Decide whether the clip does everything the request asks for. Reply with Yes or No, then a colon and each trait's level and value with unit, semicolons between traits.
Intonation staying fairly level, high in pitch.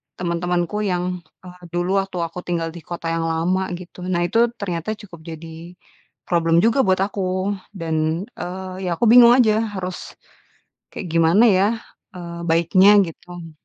No: narrow, 2.3 semitones; medium, 180 Hz